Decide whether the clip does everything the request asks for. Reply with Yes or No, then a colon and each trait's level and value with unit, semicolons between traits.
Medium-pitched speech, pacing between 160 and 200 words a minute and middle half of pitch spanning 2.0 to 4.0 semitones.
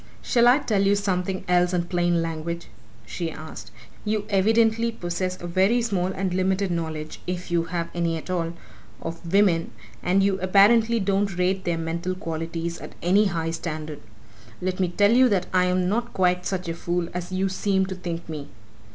Yes: medium, 180 Hz; average, 185 wpm; narrow, 2.5 semitones